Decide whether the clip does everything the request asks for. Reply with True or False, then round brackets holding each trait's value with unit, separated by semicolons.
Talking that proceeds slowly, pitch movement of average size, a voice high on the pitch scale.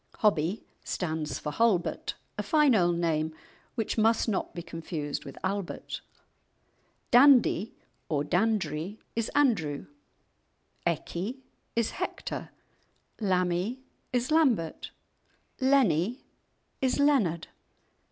False (95 wpm; 6.5 semitones; 195 Hz)